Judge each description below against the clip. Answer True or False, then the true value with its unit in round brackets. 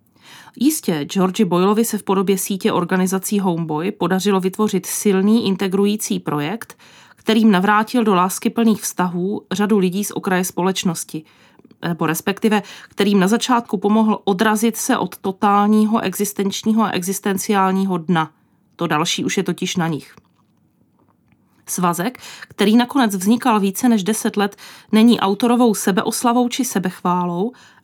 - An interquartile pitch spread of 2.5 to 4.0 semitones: True (2.9 semitones)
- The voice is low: False (200 Hz)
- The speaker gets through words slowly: False (125 wpm)